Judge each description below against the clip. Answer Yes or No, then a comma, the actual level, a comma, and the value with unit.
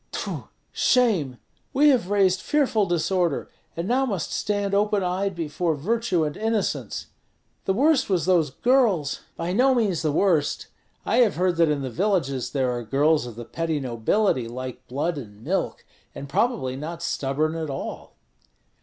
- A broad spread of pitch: Yes, wide, 6.5 semitones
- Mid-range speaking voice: Yes, medium, 170 Hz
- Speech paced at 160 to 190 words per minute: Yes, average, 165 wpm